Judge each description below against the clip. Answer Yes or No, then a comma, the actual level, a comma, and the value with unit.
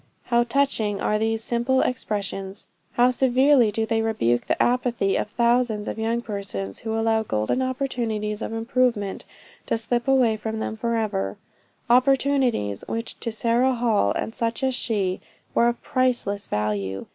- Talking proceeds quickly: No, average, 150 wpm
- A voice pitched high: Yes, high, 225 Hz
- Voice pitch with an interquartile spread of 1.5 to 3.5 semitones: Yes, average, 2.8 semitones